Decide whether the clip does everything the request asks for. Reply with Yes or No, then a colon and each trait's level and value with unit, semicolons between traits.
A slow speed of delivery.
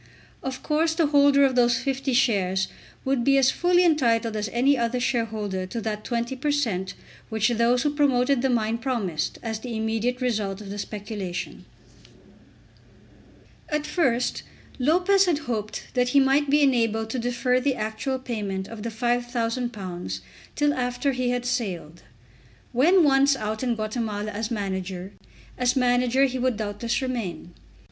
No: average, 155 wpm